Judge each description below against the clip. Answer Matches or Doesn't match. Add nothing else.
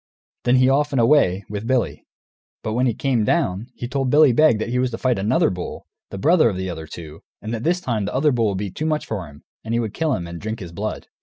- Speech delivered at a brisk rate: Matches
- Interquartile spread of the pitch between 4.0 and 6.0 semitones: Matches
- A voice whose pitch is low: Matches